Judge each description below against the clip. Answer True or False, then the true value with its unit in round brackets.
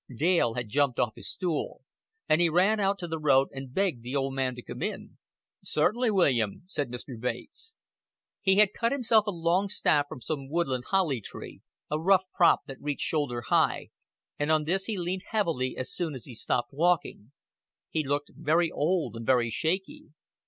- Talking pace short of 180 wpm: False (190 wpm)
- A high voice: False (155 Hz)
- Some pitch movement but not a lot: False (6.0 semitones)